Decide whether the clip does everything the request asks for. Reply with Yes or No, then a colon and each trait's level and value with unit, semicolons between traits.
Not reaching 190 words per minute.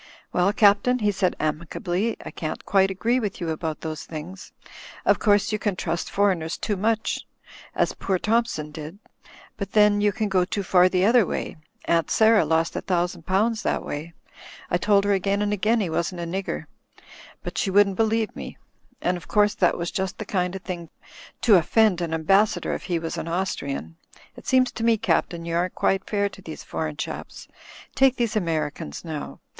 No: average, 200 wpm